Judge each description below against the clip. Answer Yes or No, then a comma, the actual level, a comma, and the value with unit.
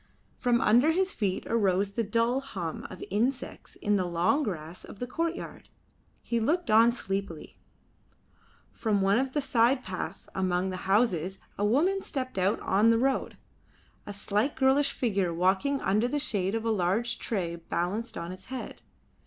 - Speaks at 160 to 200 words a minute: Yes, average, 165 wpm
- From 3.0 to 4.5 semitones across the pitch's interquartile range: No, average, 5.1 semitones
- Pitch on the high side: Yes, high, 215 Hz